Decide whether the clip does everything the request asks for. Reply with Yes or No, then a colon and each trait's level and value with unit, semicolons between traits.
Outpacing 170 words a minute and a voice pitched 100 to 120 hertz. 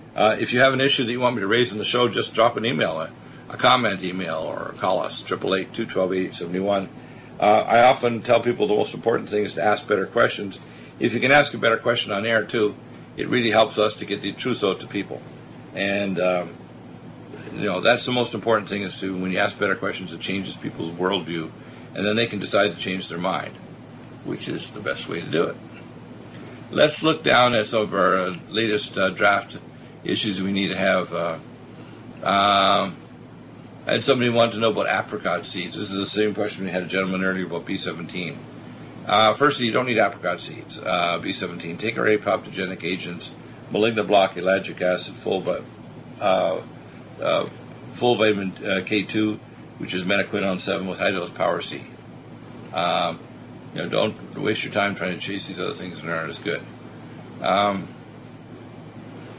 Yes: average, 190 wpm; low, 105 Hz